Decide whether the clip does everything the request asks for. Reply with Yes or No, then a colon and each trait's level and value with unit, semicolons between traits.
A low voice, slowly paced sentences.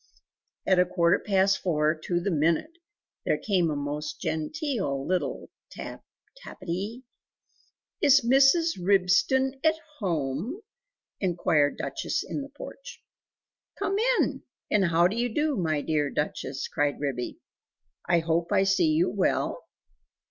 No: medium, 185 Hz; slow, 130 wpm